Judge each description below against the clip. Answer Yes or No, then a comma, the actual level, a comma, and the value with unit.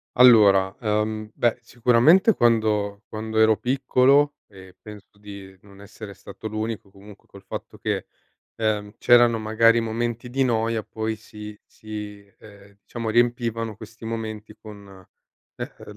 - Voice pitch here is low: Yes, low, 110 Hz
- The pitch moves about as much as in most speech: No, narrow, 2.0 semitones